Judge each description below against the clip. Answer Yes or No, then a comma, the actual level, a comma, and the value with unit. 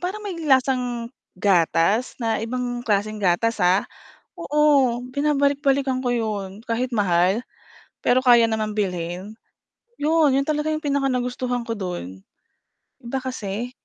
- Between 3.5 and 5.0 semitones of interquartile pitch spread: Yes, average, 4.6 semitones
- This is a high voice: Yes, high, 240 Hz